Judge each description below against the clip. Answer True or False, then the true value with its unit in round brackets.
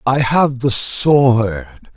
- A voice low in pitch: True (125 Hz)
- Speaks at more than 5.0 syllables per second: False (2.2 syllables/s)